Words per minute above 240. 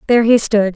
No: fast, 235 wpm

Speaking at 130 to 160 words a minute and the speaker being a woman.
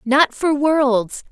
Yes: slow, 135 wpm; female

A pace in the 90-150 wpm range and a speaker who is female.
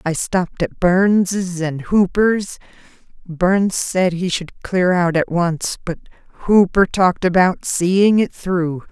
Yes: average, 140 wpm; female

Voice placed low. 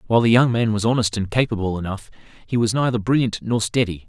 Yes: low, 110 Hz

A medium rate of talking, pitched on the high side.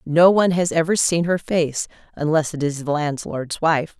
No: average, 195 wpm; medium, 160 Hz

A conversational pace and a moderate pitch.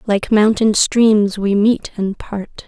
No: average, 155 wpm; high, 210 Hz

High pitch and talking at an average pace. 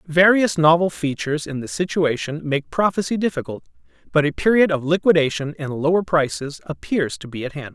No: medium, 155 Hz; average, 170 wpm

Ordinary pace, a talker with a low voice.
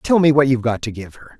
No: fast, 345 wpm; low, 130 Hz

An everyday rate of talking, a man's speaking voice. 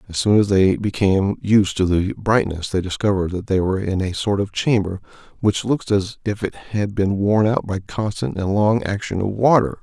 No: fast, 215 wpm; male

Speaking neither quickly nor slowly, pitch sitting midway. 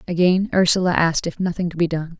No: fast, 220 wpm; medium, 175 Hz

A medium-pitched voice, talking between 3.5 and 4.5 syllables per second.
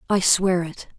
Yes: medium, 180 Hz; 4.1 syllables/s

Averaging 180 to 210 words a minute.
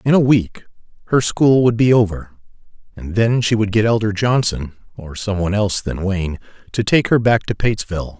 Yes: average, 200 wpm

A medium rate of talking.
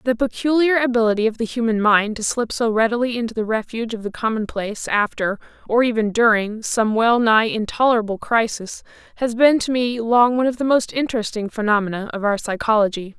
Yes: average, 180 wpm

